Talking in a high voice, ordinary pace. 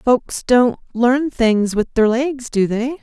Yes: high, 240 Hz; average, 180 wpm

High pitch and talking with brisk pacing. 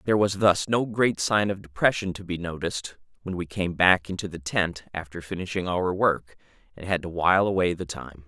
No: very low, 90 Hz; fast, 210 wpm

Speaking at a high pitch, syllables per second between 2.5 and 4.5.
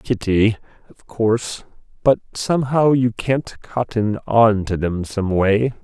No: low, 110 Hz; 4.0 syllables/s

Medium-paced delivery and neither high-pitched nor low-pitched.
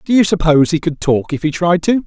No: fast, 290 wpm; medium, 170 Hz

